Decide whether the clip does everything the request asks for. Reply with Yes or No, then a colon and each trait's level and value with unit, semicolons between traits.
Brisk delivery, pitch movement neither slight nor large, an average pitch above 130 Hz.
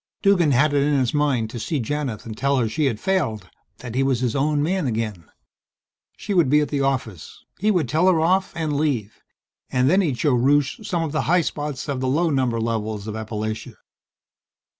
Yes: fast, 210 wpm; average, 5.0 semitones; medium, 140 Hz